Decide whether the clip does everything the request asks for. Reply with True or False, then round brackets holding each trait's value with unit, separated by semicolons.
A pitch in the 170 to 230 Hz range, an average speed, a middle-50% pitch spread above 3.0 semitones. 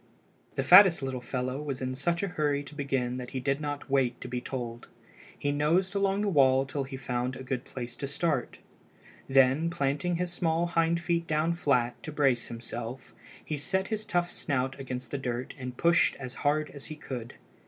False (140 Hz; 195 wpm; 4.5 semitones)